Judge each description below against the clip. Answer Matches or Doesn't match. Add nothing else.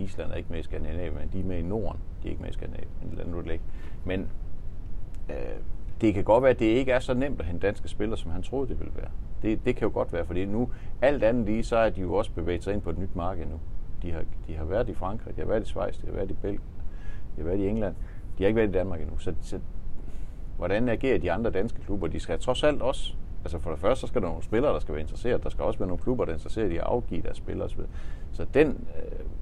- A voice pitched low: Matches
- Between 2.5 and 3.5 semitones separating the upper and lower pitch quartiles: Doesn't match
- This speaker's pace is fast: Matches